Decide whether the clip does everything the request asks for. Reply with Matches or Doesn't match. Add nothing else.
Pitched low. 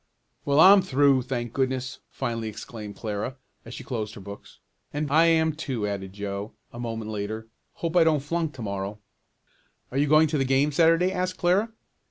Matches